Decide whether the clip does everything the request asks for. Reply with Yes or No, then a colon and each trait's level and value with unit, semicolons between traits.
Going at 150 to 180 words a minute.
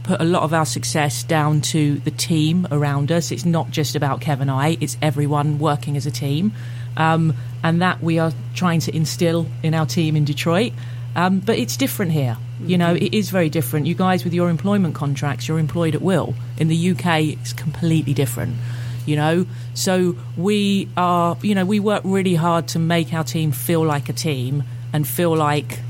No: average, 200 wpm